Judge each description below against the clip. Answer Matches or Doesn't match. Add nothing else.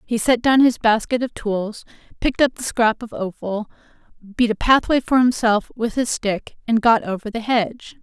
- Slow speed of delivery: Doesn't match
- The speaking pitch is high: Matches